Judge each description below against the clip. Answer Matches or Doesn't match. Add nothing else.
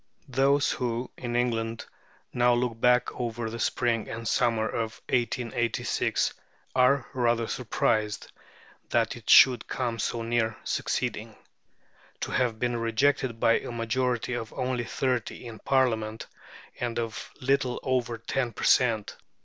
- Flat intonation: Matches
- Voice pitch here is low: Matches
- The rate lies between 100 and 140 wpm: Matches